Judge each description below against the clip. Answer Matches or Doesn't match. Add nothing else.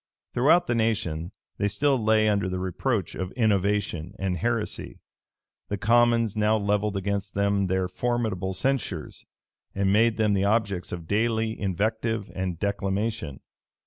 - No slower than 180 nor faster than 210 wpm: Doesn't match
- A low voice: Matches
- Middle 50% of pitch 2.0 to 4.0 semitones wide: Matches